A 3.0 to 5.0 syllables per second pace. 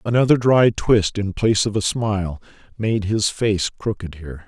Yes: 4.9 syllables/s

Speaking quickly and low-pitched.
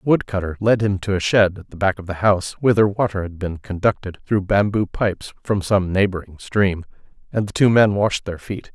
Yes: fast, 220 wpm; low, 100 Hz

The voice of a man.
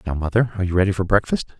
Yes: male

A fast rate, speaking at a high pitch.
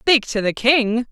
Yes: fast, 215 wpm; high, 240 Hz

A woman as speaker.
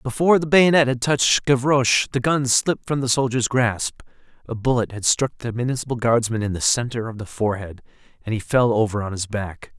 No: male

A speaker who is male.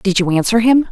No: female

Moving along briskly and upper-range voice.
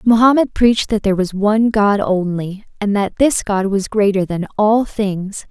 No: average, 185 wpm; high, 205 Hz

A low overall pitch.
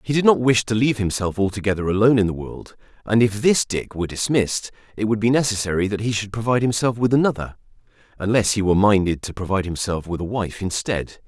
Yes: low, 105 Hz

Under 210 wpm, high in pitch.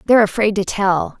Yes: average, 200 wpm; high, 200 Hz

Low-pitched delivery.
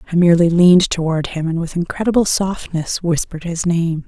No: medium, 170 Hz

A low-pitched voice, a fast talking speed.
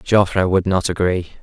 No: very low, 95 Hz; average, 170 wpm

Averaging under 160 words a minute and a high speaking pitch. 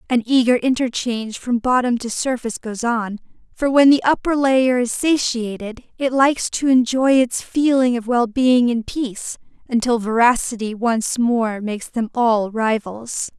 Yes: average, 150 wpm; high, 240 Hz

